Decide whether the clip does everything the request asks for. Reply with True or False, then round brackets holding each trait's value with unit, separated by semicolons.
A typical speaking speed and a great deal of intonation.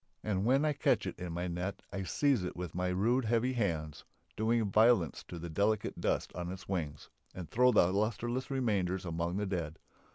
False (195 wpm; 4.7 semitones)